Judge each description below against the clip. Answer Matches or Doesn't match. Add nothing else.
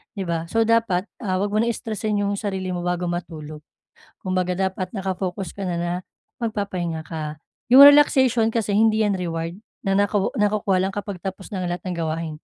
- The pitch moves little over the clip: Doesn't match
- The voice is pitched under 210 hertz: Matches